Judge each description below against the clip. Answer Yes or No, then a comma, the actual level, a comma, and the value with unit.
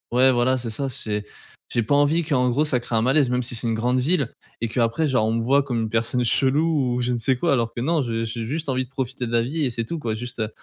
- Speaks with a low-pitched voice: Yes, low, 125 Hz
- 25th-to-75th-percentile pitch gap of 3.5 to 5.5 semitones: No, average, 2.9 semitones